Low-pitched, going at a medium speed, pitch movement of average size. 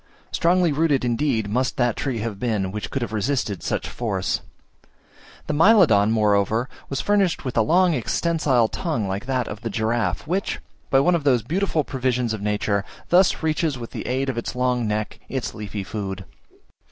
No: low, 125 Hz; average, 175 wpm; wide, 5.8 semitones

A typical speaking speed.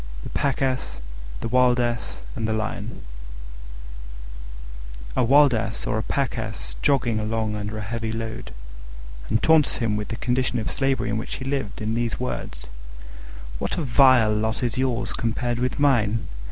Yes: average, 165 wpm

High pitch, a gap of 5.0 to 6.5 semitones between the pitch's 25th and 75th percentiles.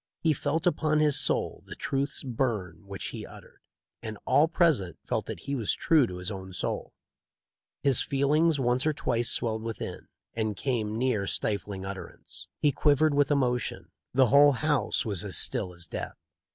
No: low, 125 Hz; wide, 5.6 semitones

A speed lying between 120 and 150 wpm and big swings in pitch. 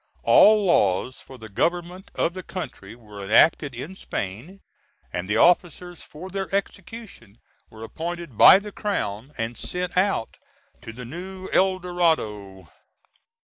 Yes: average, 140 wpm; wide, 8.7 semitones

